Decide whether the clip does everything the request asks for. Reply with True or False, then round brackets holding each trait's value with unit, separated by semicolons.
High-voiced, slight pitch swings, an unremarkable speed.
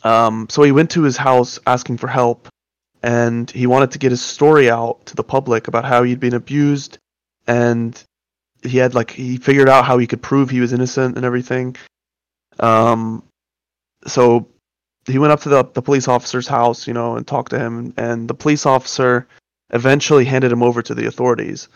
False (125 Hz; 2.0 semitones; 195 wpm)